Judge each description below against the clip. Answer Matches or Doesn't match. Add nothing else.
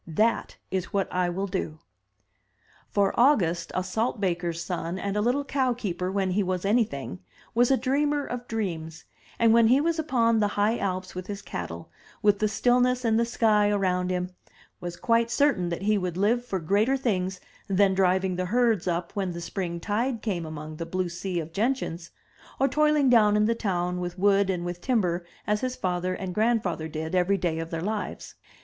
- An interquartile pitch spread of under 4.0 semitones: Doesn't match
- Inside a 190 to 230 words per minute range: Matches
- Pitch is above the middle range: Matches